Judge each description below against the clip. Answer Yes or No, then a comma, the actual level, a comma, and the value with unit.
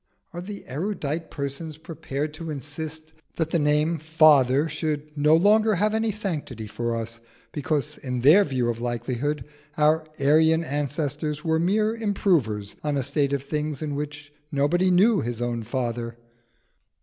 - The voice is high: No, medium, 150 Hz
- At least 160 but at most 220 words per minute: No, average, 150 wpm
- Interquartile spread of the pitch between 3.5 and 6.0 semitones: No, average, 3.0 semitones